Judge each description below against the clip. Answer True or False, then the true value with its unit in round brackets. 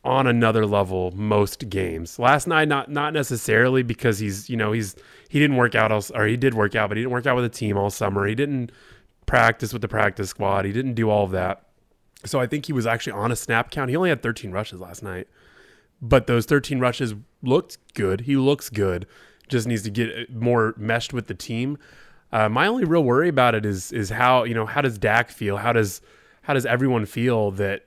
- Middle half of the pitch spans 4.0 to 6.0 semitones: False (3.5 semitones)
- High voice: False (115 Hz)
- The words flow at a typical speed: False (230 wpm)